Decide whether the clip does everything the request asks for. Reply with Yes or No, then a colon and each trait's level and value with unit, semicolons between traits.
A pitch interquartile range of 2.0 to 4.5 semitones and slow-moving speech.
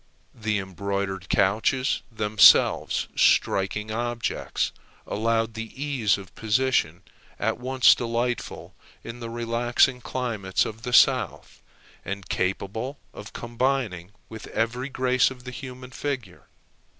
Yes: average, 3.7 semitones; slow, 115 wpm